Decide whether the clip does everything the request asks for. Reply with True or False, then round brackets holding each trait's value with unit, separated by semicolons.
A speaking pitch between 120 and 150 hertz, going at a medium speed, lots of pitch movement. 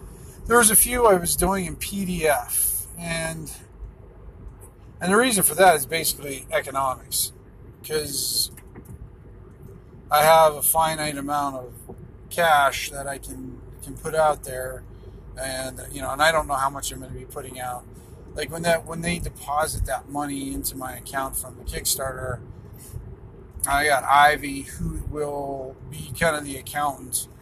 False (135 Hz; 155 wpm; 3.6 semitones)